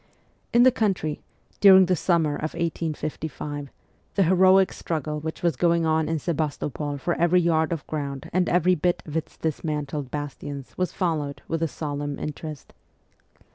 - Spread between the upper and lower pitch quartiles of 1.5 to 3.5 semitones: Yes, average, 2.8 semitones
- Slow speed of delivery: No, average, 155 wpm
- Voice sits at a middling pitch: Yes, medium, 160 Hz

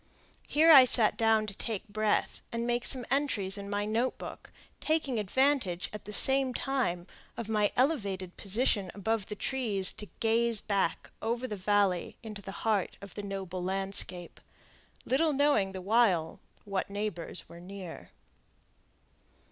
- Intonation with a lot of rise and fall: No, average, 3.7 semitones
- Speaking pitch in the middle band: No, high, 210 Hz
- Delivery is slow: No, average, 150 wpm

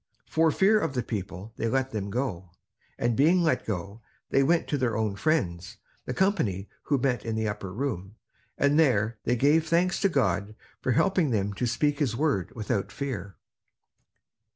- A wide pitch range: Yes, wide, 6.2 semitones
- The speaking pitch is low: Yes, low, 120 Hz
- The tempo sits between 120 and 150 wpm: No, average, 175 wpm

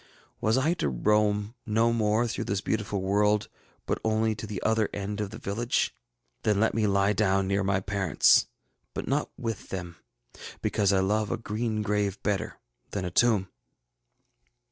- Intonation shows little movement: Yes, narrow, 1.8 semitones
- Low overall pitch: Yes, low, 105 Hz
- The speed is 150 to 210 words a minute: Yes, average, 165 wpm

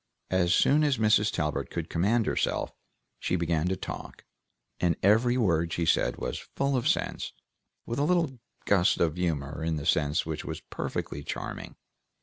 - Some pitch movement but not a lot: No, wide, 6.4 semitones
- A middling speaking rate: Yes, average, 165 wpm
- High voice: No, very low, 90 Hz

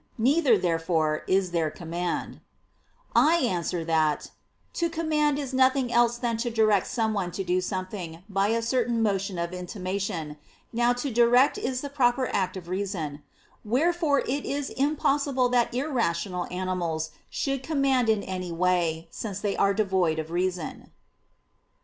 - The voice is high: Yes, high, 205 Hz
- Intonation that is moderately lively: No, wide, 6.2 semitones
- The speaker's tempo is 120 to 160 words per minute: Yes, average, 145 wpm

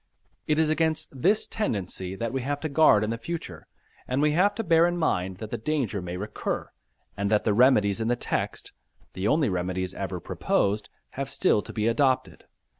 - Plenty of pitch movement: Yes, wide, 7.4 semitones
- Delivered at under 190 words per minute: No, average, 195 wpm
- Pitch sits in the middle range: No, low, 120 Hz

